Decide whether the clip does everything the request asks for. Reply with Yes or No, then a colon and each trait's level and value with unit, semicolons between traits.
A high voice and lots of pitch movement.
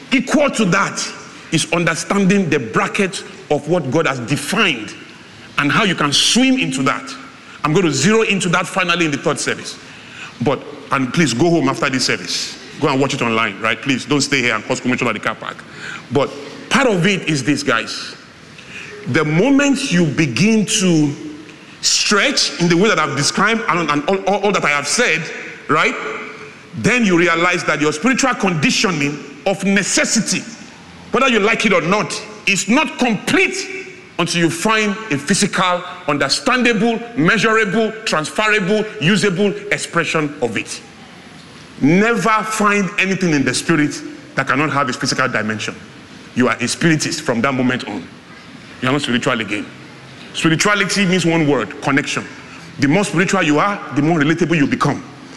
No: medium, 175 Hz; wide, 6.3 semitones